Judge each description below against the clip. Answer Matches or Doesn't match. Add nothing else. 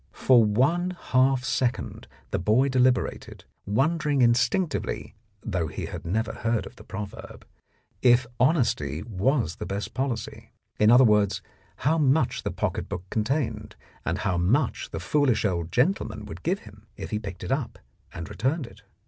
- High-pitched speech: Doesn't match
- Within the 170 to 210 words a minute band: Doesn't match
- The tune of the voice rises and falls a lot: Doesn't match